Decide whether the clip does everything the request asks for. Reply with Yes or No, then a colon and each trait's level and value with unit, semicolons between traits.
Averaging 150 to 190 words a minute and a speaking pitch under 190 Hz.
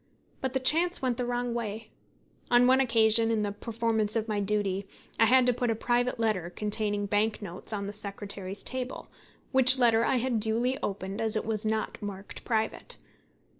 No: average, 185 wpm; high, 225 Hz